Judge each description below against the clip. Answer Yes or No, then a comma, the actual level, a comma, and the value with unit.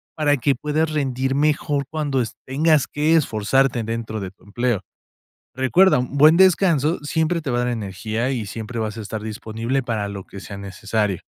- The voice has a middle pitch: No, low, 125 Hz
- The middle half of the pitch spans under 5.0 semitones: No, average, 5.3 semitones